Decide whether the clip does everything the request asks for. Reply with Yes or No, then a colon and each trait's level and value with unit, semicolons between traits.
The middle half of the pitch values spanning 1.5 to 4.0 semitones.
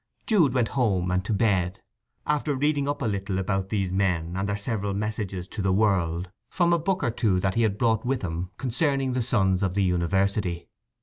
No: average, 4.8 semitones